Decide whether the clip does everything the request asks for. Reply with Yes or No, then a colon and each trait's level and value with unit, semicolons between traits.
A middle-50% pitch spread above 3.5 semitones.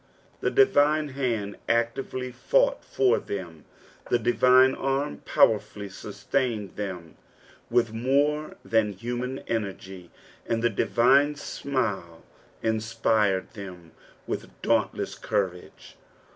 Yes: average, 4.8 semitones